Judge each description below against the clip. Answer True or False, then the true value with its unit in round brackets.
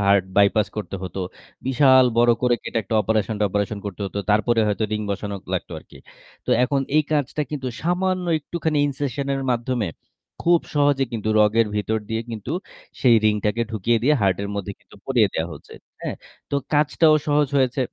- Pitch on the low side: True (115 Hz)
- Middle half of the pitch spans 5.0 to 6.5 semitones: True (5.3 semitones)